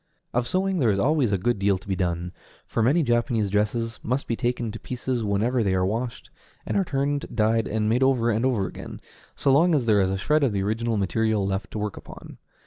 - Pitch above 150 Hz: No, low, 115 Hz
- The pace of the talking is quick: Yes, fast, 230 wpm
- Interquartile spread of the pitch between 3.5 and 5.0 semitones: Yes, average, 3.9 semitones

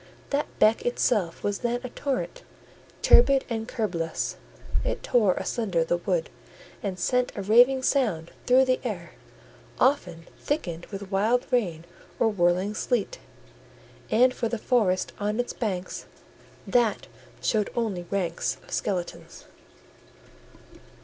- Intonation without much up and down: No, average, 5.2 semitones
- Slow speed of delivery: Yes, slow, 125 wpm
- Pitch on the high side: Yes, high, 215 Hz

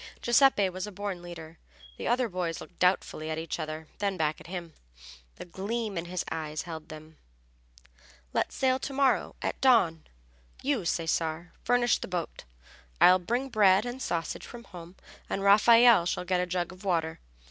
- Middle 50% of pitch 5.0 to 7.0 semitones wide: Yes, wide, 5.4 semitones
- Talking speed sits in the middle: Yes, average, 170 wpm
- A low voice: No, medium, 180 Hz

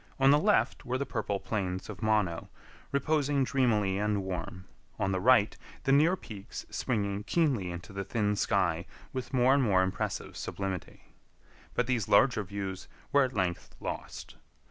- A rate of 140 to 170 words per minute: Yes, average, 160 wpm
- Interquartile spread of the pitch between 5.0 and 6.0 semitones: Yes, average, 5.3 semitones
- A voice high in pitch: No, low, 105 Hz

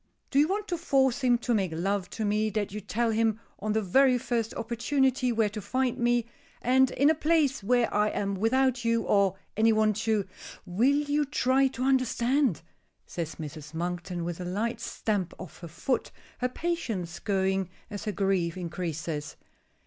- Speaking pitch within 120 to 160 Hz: No, high, 220 Hz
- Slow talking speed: No, average, 180 wpm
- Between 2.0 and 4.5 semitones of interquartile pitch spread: No, average, 5.1 semitones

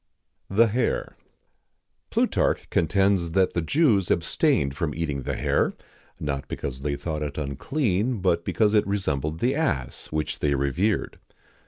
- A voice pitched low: Yes, very low, 85 Hz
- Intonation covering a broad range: Yes, wide, 6.2 semitones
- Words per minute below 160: Yes, average, 145 wpm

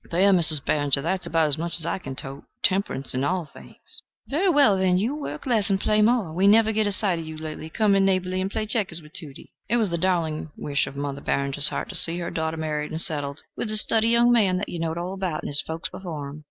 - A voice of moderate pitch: Yes, medium, 175 Hz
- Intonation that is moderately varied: Yes, average, 4.7 semitones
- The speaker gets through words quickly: Yes, fast, 260 wpm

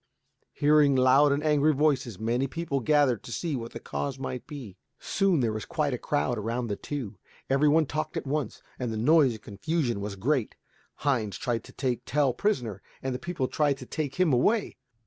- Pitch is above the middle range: No, low, 135 Hz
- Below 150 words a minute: No, average, 200 wpm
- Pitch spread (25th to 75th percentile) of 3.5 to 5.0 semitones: Yes, average, 4.1 semitones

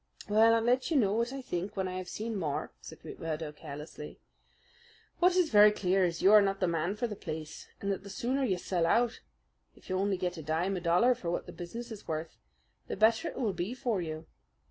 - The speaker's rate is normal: No, fast, 235 wpm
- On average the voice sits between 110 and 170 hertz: No, high, 195 Hz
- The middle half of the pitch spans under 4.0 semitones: No, average, 4.9 semitones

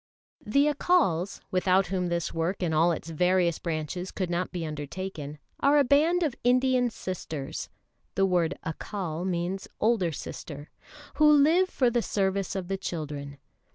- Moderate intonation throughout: No, wide, 6.4 semitones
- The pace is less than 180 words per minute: Yes, average, 155 wpm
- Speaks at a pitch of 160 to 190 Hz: Yes, medium, 185 Hz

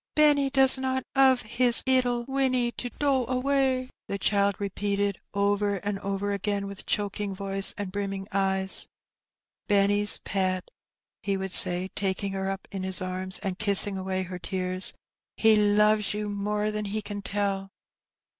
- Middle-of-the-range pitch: No, high, 205 Hz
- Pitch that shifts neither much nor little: No, narrow, 2.2 semitones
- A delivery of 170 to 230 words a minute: No, average, 155 wpm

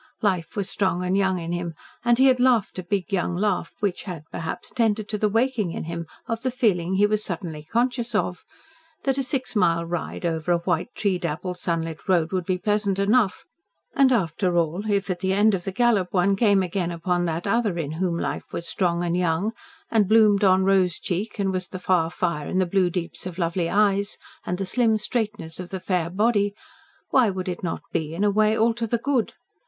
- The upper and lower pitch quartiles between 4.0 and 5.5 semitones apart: No, average, 3.5 semitones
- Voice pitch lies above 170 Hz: Yes, high, 190 Hz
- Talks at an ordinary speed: No, fast, 220 wpm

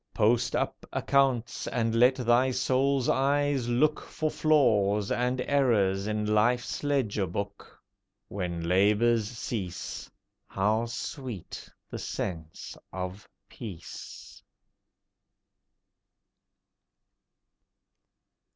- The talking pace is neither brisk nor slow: No, slow, 85 wpm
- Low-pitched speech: Yes, low, 115 Hz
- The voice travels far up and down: No, average, 4.3 semitones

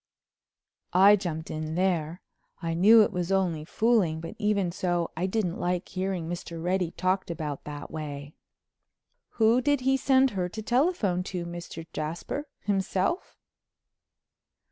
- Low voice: No, medium, 180 Hz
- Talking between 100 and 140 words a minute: Yes, slow, 135 wpm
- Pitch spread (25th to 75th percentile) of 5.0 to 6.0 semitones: No, average, 4.0 semitones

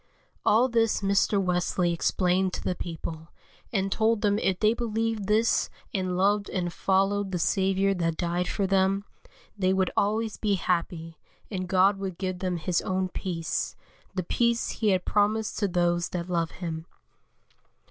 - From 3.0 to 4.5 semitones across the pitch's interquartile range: No, narrow, 2.5 semitones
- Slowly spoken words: No, average, 160 wpm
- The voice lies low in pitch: No, high, 190 Hz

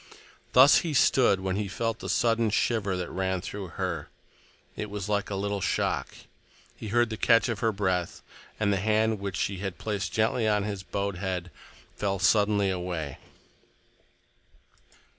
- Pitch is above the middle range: No, low, 100 Hz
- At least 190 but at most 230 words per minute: No, average, 160 wpm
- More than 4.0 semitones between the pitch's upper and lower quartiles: No, narrow, 2.6 semitones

